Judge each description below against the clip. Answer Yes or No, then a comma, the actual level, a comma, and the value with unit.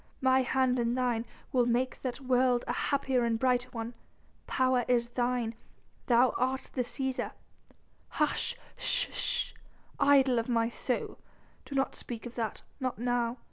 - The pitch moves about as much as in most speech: No, narrow, 1.5 semitones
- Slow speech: No, average, 150 wpm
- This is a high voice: Yes, very high, 250 Hz